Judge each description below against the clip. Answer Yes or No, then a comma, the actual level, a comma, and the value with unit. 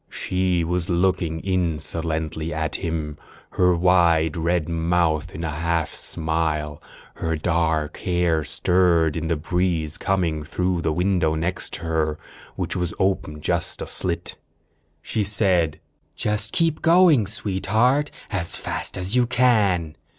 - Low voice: Yes, very low, 85 Hz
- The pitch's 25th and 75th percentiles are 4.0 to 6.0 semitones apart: No, average, 2.8 semitones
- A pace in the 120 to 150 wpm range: Yes, slow, 135 wpm